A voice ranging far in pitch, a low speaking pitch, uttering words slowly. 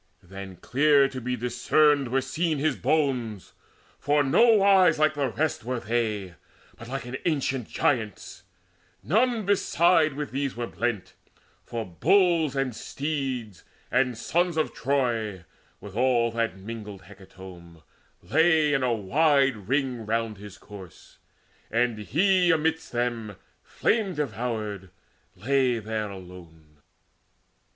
Yes: wide, 5.8 semitones; low, 125 Hz; slow, 125 wpm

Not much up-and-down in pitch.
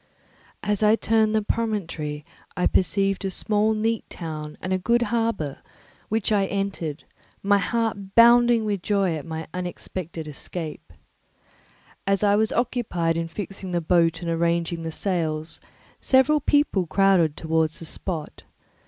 No: average, 4.6 semitones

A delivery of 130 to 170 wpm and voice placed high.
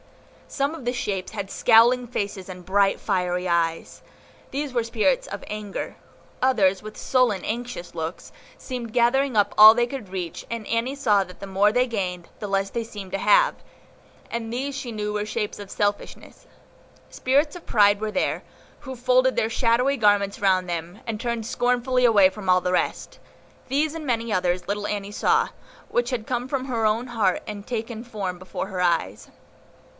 No: average, 180 wpm; high, 215 Hz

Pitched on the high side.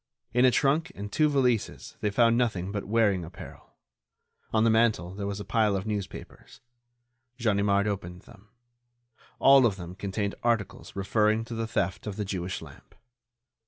No: low, 105 Hz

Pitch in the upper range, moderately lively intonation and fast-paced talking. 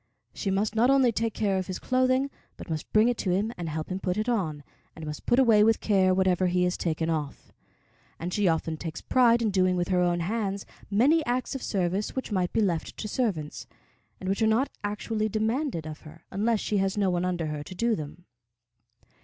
Yes: high, 195 Hz; average, 4.4 semitones; fast, 220 wpm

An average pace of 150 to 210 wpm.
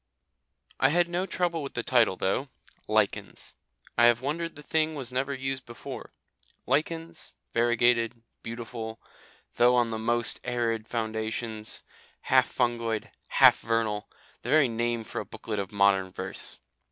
No: average, 140 wpm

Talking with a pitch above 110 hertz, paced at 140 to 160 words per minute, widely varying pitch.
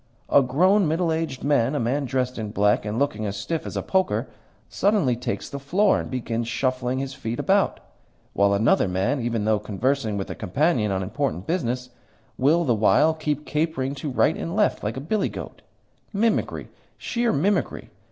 No: low, 135 Hz; average, 180 wpm; wide, 6.0 semitones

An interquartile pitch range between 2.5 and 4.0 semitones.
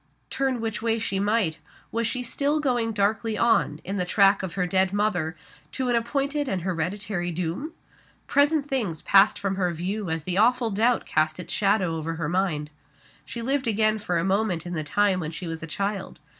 No: average, 4.7 semitones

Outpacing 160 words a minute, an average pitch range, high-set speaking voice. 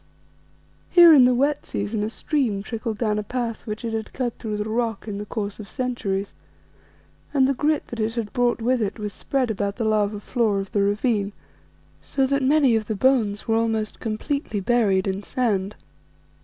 Yes: average, 195 wpm; average, 3.3 semitones; high, 225 Hz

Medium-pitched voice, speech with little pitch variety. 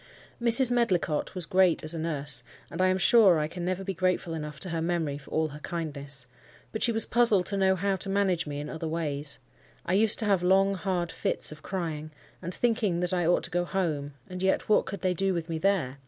No: medium, 175 Hz; average, 3.6 semitones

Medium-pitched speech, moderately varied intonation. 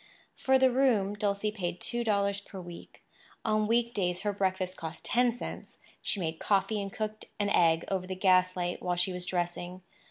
No: high, 195 Hz; average, 3.0 semitones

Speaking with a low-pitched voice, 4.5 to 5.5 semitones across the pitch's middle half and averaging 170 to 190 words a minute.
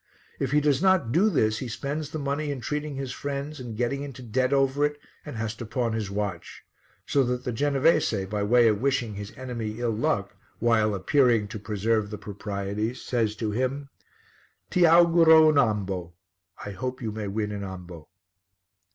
Yes: low, 120 Hz; average, 4.9 semitones; average, 185 wpm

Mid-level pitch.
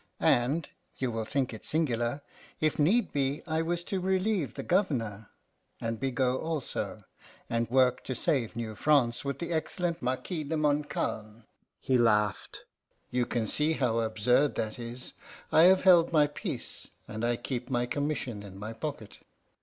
No: low, 130 Hz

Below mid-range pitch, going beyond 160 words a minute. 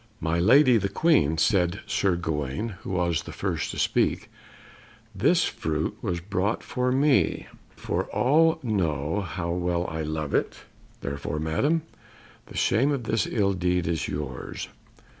No: very low, 90 Hz; average, 145 wpm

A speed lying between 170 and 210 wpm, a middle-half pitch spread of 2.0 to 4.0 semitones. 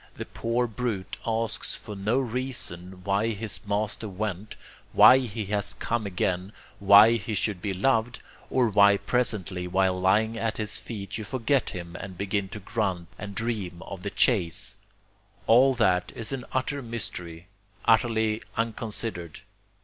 No: average, 150 wpm; average, 3.2 semitones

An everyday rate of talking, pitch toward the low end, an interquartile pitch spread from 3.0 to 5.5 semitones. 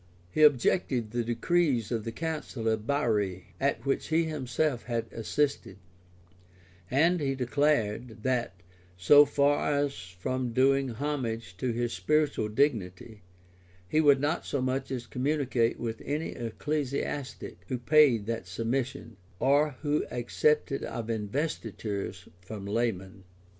No: slow, 125 wpm; low, 125 Hz; average, 4.4 semitones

